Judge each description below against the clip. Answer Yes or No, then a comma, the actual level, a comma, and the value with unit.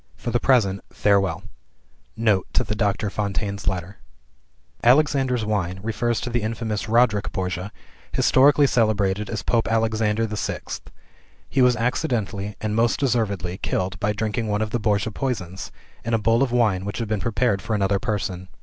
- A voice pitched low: Yes, low, 110 Hz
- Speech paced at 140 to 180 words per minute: Yes, average, 160 wpm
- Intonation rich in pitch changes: No, average, 2.8 semitones